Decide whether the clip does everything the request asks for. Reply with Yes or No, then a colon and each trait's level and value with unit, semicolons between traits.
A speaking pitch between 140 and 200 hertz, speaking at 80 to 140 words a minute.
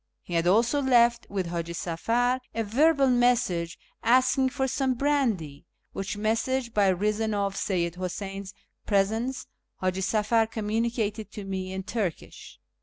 No: high, 215 Hz; slow, 135 wpm